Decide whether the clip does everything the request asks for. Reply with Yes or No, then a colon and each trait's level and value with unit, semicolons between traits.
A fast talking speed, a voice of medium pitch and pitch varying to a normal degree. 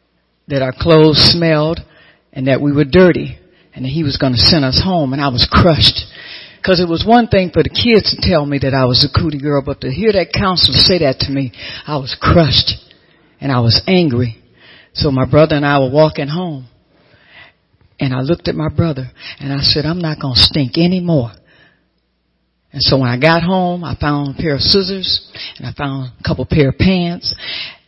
Yes: fast, 210 wpm; medium, 145 Hz; average, 4.1 semitones